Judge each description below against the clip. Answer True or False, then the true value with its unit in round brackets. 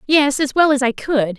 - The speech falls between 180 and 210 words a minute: False (260 wpm)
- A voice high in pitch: True (270 Hz)